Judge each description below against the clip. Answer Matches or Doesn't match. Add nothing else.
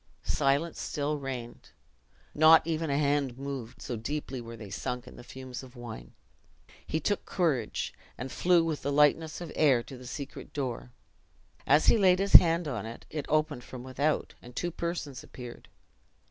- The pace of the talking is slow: Doesn't match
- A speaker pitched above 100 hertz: Matches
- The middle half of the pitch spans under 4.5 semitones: Matches